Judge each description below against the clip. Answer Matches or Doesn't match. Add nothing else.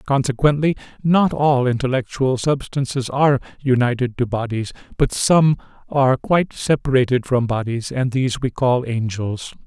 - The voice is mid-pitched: Doesn't match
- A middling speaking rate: Doesn't match